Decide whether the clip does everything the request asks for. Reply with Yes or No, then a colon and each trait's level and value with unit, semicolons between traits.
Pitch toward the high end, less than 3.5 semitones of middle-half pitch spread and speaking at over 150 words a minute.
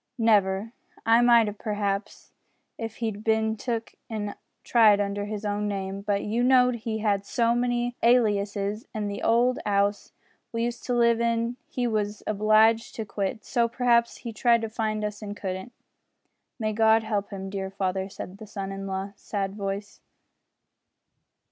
Yes: high, 215 Hz; narrow, 2.5 semitones; average, 165 wpm